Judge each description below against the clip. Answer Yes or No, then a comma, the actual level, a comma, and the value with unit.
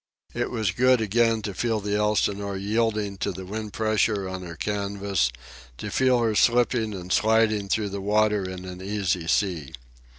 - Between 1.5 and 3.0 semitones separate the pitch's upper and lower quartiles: Yes, narrow, 2.4 semitones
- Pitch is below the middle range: Yes, low, 105 Hz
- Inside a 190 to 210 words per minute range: No, average, 175 wpm